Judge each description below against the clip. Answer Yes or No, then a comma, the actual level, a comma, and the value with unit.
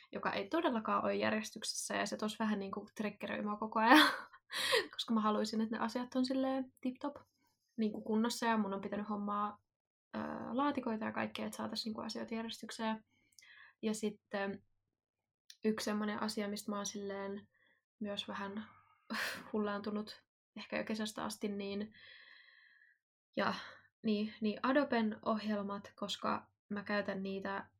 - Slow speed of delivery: No, average, 135 wpm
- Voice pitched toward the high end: Yes, high, 215 Hz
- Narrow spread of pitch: Yes, narrow, 2.1 semitones